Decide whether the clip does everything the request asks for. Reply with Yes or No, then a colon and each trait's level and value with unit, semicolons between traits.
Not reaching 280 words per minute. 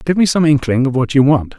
No: fast, 305 wpm